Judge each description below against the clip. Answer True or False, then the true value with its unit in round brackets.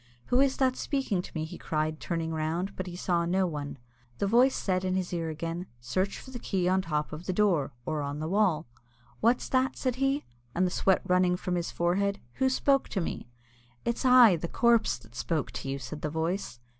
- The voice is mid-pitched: True (180 Hz)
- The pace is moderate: False (220 wpm)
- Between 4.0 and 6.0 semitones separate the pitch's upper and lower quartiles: True (5.0 semitones)